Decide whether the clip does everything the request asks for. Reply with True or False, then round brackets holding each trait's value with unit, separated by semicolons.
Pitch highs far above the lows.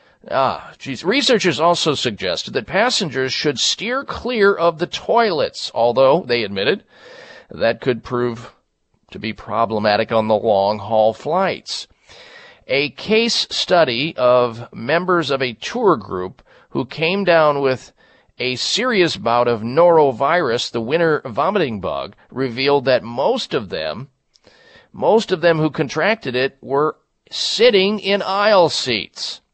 True (8.3 semitones)